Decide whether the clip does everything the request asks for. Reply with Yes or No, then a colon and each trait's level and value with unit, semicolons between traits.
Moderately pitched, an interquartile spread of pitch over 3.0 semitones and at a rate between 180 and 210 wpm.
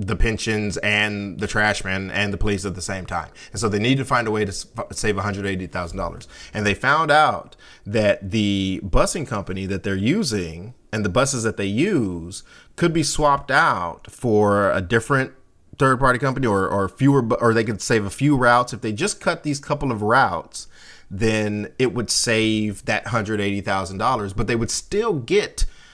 No: low, 105 Hz; average, 3.7 semitones; average, 195 wpm